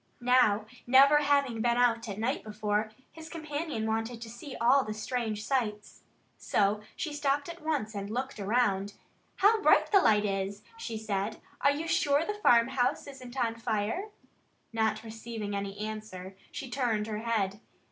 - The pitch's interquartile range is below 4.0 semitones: No, average, 4.4 semitones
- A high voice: Yes, high, 230 Hz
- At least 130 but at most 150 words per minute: No, average, 160 wpm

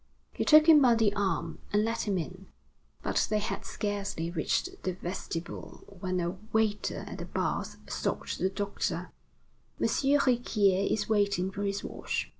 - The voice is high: Yes, high, 200 Hz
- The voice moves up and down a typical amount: Yes, average, 3.0 semitones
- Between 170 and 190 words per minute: No, average, 160 wpm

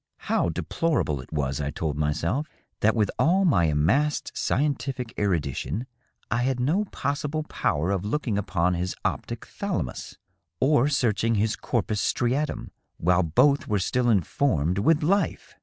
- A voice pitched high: No, low, 110 Hz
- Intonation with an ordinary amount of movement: No, wide, 8.8 semitones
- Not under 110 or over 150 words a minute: Yes, average, 145 wpm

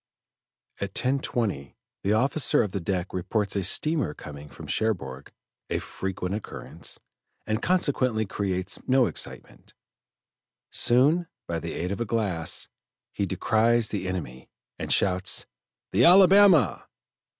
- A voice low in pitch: Yes, low, 105 Hz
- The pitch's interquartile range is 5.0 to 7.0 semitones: Yes, wide, 5.5 semitones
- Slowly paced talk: Yes, slow, 125 wpm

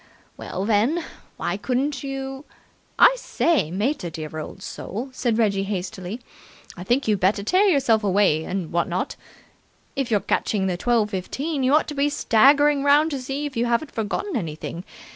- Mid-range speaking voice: No, high, 230 Hz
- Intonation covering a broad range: Yes, wide, 6.3 semitones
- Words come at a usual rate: Yes, average, 170 wpm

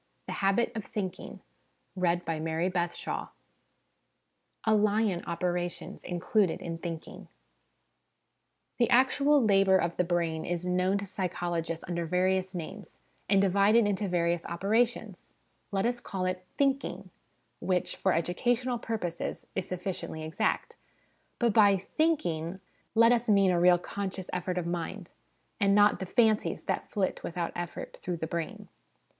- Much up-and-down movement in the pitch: No, average, 3.3 semitones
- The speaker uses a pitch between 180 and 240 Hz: Yes, medium, 185 Hz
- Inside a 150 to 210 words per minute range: No, slow, 135 wpm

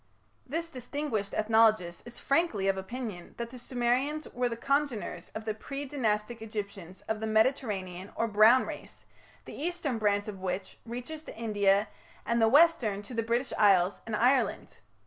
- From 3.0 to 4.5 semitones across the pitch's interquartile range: Yes, average, 3.9 semitones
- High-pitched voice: Yes, high, 225 Hz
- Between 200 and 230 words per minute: No, average, 165 wpm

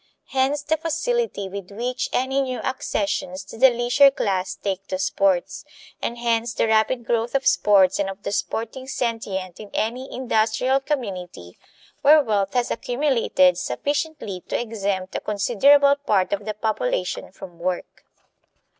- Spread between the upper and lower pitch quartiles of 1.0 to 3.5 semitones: No, average, 5.2 semitones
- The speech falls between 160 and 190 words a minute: No, average, 145 wpm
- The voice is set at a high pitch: Yes, high, 225 Hz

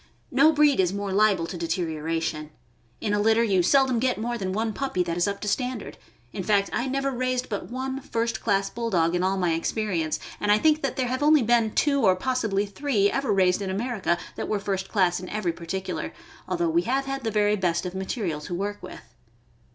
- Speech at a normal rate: No, fast, 215 wpm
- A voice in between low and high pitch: No, high, 205 Hz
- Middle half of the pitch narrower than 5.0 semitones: No, wide, 5.4 semitones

